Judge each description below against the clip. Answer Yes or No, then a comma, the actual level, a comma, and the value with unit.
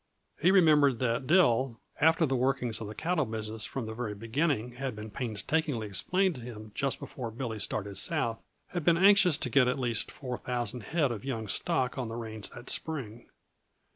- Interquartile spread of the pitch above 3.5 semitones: Yes, average, 4.9 semitones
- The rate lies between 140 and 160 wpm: No, average, 190 wpm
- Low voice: Yes, low, 125 Hz